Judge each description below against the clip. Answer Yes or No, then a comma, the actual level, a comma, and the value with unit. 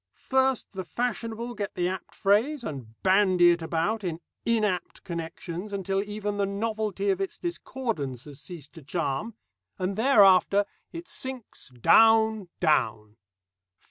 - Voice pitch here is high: Yes, high, 195 Hz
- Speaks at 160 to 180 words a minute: No, slow, 135 wpm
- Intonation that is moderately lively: Yes, average, 4.5 semitones